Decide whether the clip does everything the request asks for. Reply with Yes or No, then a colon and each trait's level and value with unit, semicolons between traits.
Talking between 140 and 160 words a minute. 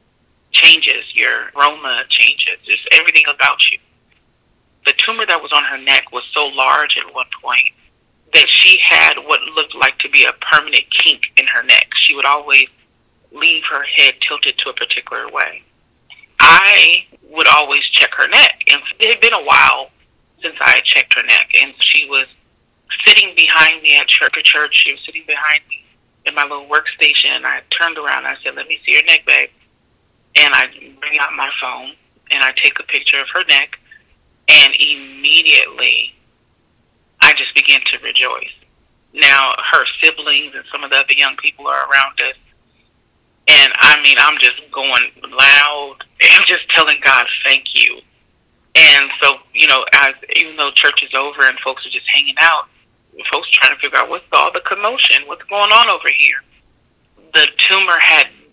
No: average, 180 wpm